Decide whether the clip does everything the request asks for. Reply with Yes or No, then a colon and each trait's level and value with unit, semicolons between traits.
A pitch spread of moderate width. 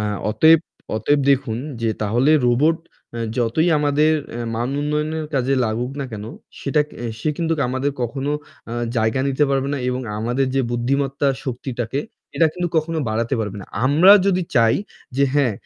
Yes: average, 4.0 semitones